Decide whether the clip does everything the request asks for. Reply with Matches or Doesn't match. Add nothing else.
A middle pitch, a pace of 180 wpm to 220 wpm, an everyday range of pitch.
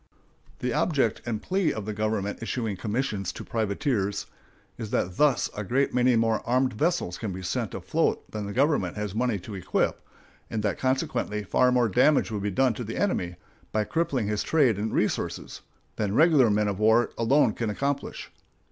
Doesn't match